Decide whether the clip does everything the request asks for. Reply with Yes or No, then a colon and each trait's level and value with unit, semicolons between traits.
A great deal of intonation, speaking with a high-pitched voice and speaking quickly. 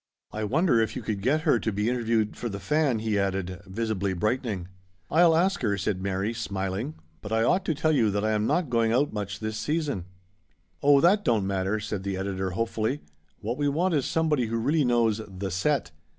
No: wide, 6.0 semitones; low, 110 Hz; fast, 220 wpm